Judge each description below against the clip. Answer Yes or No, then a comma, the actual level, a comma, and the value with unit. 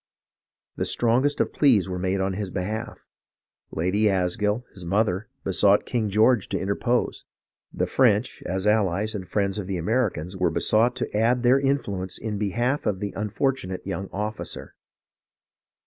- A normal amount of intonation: Yes, average, 3.4 semitones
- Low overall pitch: Yes, low, 105 Hz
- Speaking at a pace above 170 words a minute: No, average, 150 wpm